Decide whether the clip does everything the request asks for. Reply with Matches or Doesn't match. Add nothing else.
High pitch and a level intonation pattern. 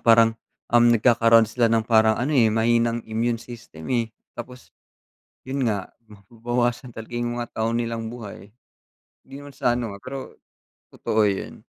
Doesn't match